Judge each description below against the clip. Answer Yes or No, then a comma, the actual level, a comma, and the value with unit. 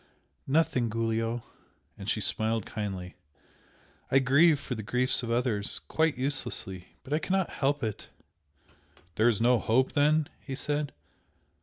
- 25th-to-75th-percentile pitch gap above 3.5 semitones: Yes, average, 4.5 semitones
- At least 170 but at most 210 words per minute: No, average, 140 wpm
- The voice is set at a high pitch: No, low, 125 Hz